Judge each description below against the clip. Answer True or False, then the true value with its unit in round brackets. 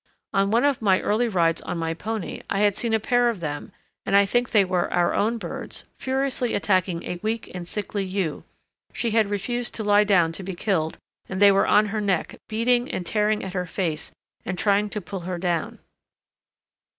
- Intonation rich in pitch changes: False (3.5 semitones)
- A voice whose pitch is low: False (200 Hz)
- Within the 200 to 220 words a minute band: True (205 wpm)